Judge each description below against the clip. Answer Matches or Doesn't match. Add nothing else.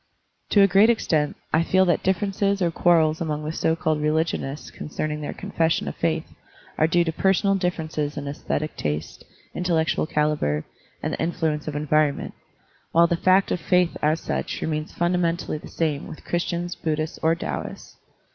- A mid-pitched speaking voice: Matches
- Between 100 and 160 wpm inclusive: Doesn't match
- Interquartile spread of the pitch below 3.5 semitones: Matches